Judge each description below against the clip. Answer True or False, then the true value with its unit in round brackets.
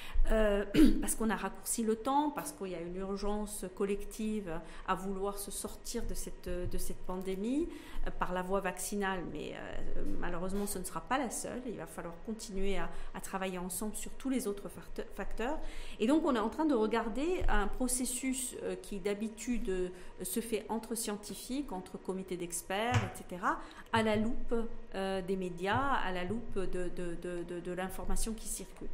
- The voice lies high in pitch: True (200 Hz)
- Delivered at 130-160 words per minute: False (180 wpm)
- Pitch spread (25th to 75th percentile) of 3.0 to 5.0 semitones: True (3.3 semitones)